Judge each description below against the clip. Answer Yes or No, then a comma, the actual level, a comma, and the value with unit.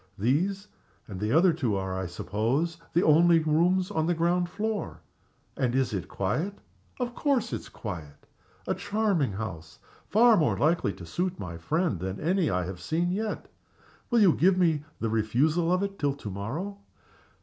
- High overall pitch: No, medium, 160 Hz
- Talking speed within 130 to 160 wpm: No, average, 170 wpm